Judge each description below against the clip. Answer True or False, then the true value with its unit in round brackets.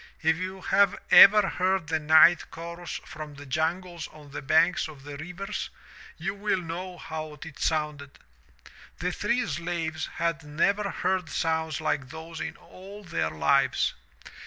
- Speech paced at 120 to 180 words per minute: True (150 wpm)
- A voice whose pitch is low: False (165 Hz)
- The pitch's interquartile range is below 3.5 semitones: True (2.8 semitones)